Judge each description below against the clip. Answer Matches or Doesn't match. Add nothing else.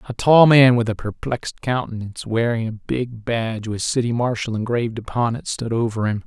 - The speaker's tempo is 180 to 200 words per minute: Matches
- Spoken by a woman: Doesn't match